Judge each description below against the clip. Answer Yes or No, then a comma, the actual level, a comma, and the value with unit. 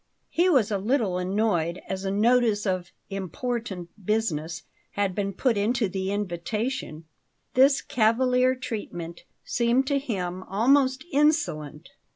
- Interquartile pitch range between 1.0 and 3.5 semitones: No, wide, 5.4 semitones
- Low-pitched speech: No, high, 210 Hz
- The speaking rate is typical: No, slow, 125 wpm